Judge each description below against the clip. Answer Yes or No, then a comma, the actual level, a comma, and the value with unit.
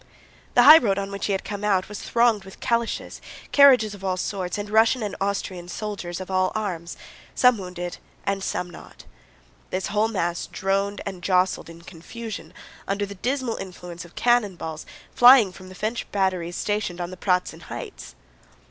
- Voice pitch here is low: No, high, 195 Hz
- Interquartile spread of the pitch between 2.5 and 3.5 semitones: Yes, average, 2.9 semitones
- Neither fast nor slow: Yes, average, 175 wpm